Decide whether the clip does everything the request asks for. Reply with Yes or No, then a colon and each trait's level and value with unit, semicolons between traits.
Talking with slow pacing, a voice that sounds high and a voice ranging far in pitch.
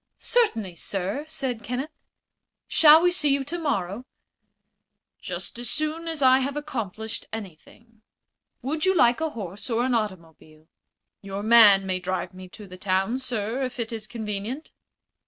No: average, 150 wpm; high, 230 Hz; wide, 6.1 semitones